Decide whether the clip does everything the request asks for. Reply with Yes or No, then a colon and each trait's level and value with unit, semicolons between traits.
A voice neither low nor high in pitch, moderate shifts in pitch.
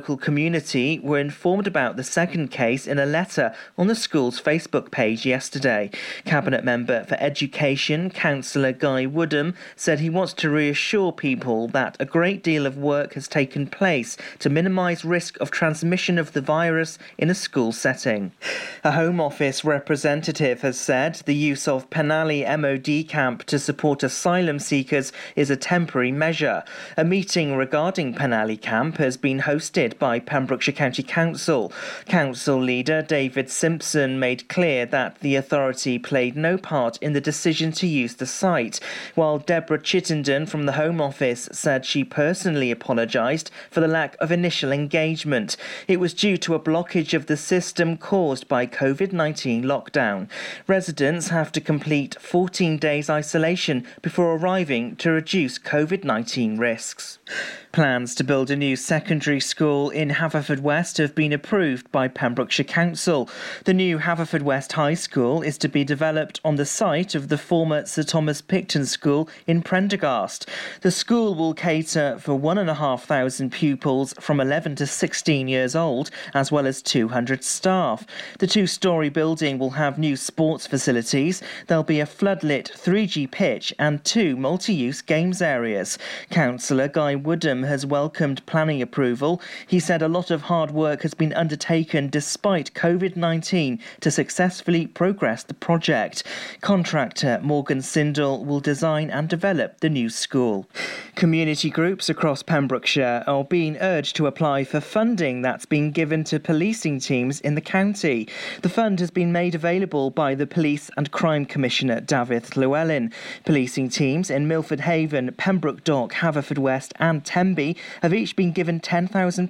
Yes: medium, 155 Hz; average, 3.5 semitones